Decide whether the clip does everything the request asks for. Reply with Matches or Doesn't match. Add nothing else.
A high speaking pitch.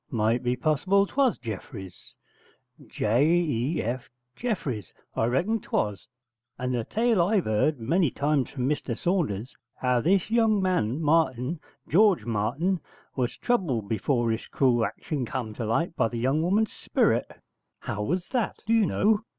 Doesn't match